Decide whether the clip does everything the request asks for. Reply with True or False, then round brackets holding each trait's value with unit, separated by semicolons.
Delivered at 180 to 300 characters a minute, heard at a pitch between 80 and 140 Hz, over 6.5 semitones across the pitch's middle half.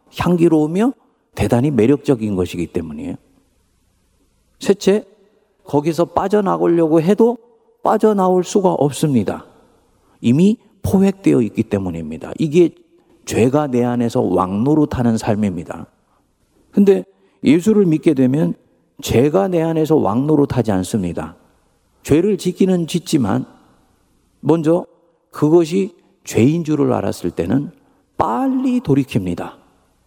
False (255 characters per minute; 155 Hz; 8.9 semitones)